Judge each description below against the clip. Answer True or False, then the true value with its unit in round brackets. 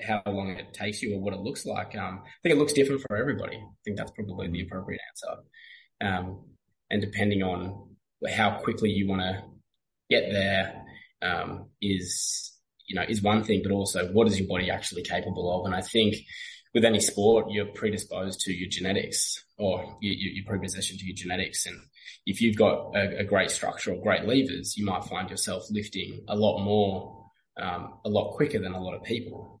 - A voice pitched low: True (100 Hz)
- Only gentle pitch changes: True (2.0 semitones)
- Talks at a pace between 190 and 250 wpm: True (200 wpm)